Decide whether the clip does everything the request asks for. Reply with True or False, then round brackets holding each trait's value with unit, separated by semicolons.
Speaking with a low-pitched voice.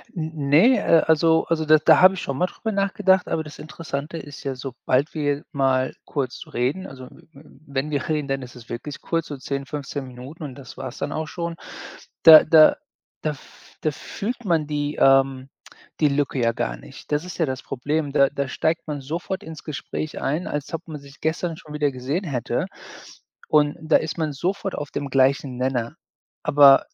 False (145 Hz)